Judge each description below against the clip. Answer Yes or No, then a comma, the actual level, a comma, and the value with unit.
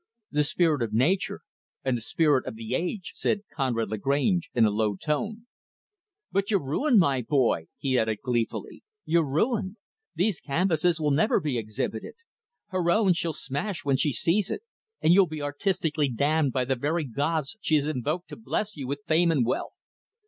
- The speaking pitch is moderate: Yes, medium, 150 Hz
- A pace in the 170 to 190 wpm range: Yes, average, 180 wpm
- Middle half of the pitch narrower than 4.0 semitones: No, wide, 5.5 semitones